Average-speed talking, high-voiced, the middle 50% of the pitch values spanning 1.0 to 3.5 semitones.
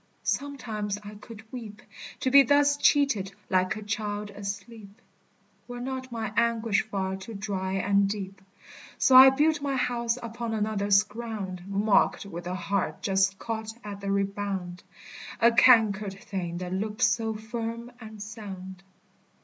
Yes: average, 145 wpm; high, 210 Hz; average, 2.9 semitones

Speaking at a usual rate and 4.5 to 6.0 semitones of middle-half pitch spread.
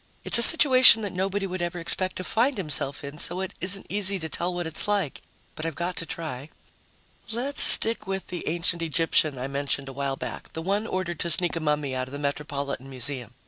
No: fast, 220 wpm; average, 5.2 semitones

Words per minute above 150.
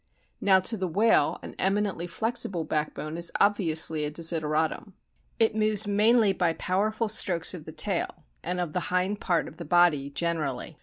Yes: average, 165 wpm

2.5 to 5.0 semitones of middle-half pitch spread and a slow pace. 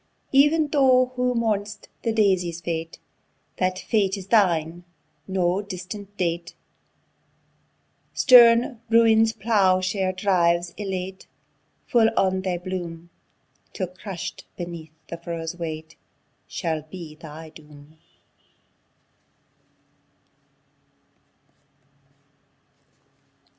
Yes: average, 4.1 semitones; slow, 85 wpm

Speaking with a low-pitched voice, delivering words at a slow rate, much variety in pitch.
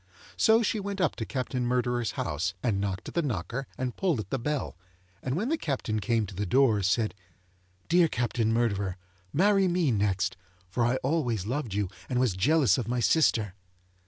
No: low, 120 Hz; average, 190 wpm; wide, 6.3 semitones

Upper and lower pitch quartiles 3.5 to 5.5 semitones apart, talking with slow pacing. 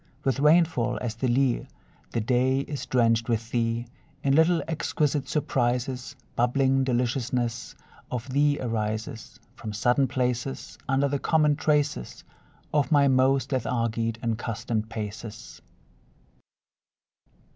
No: average, 3.1 semitones; slow, 115 wpm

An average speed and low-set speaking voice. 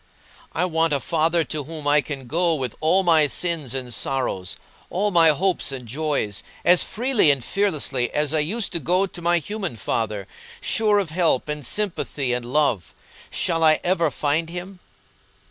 No: average, 175 wpm; medium, 155 Hz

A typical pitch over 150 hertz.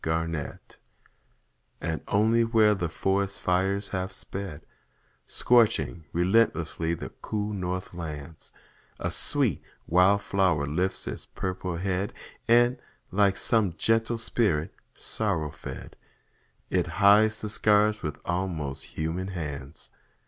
No: very low, 95 Hz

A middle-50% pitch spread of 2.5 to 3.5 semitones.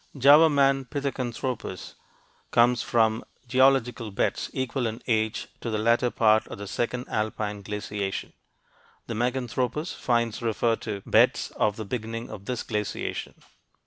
Yes: average, 2.8 semitones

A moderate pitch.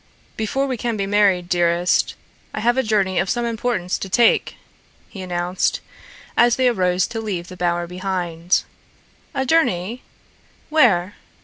No: high, 195 Hz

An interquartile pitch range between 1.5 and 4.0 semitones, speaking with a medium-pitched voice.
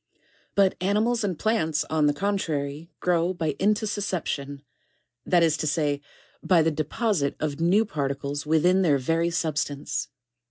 No: average, 4.7 semitones; medium, 165 Hz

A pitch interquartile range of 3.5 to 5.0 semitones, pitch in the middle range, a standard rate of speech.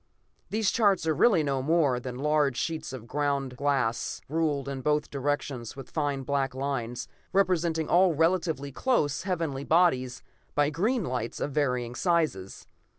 Yes: average, 3.9 semitones; medium, 145 Hz; average, 150 wpm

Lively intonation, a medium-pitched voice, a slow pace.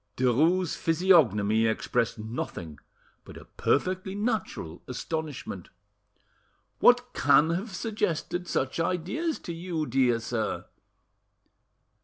Yes: wide, 7.4 semitones; medium, 160 Hz; slow, 95 wpm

